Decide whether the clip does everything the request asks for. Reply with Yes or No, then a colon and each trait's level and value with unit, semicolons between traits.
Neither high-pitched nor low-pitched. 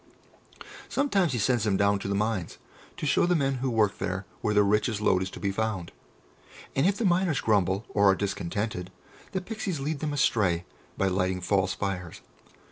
No: low, 105 Hz